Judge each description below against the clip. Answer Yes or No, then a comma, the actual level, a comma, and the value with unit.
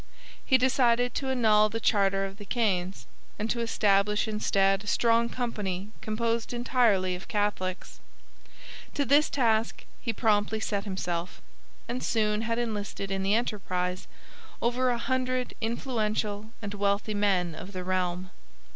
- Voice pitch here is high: Yes, high, 210 Hz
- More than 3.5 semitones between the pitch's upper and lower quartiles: No, average, 3.2 semitones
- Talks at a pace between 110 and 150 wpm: Yes, average, 140 wpm